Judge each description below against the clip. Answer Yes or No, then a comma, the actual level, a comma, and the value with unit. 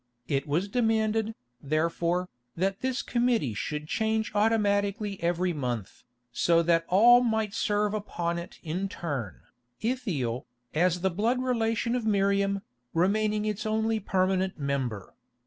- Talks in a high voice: Yes, high, 195 Hz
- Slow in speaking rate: Yes, slow, 130 wpm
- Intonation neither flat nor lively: Yes, average, 4.7 semitones